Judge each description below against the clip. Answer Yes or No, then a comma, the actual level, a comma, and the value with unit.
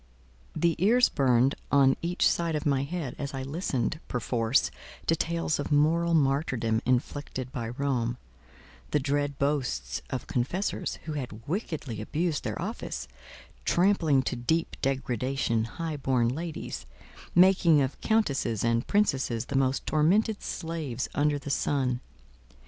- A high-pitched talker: No, medium, 140 Hz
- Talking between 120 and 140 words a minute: Yes, slow, 135 wpm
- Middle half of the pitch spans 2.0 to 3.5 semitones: No, average, 4.5 semitones